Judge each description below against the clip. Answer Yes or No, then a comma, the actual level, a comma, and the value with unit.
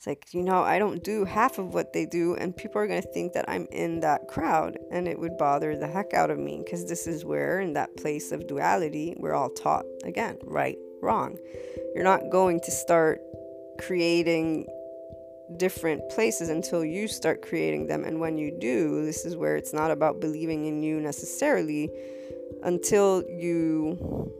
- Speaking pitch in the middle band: Yes, medium, 160 Hz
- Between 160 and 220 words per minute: Yes, average, 185 wpm